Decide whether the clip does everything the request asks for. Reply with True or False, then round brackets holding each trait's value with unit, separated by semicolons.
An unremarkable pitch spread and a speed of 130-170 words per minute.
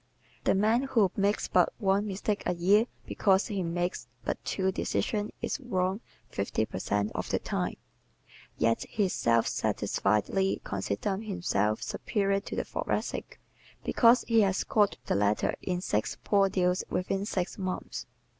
True (3.1 semitones; 150 wpm)